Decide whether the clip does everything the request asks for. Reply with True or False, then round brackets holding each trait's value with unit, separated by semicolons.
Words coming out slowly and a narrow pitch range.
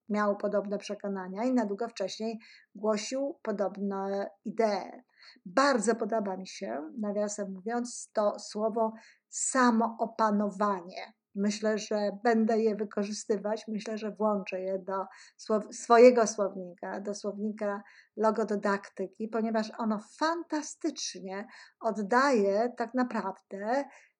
True (100 wpm; 2.2 semitones)